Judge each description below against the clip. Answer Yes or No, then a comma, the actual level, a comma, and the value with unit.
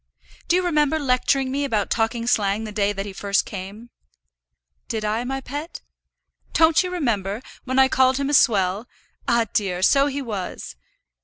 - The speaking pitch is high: Yes, high, 240 Hz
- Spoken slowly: No, average, 170 wpm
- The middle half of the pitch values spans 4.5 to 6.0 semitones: Yes, average, 5.1 semitones